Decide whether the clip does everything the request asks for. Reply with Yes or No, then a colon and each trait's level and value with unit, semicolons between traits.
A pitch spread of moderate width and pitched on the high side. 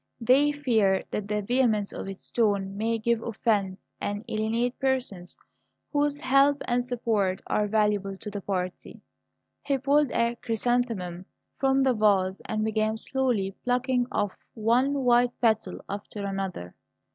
Yes: average, 3.7 semitones; high, 220 Hz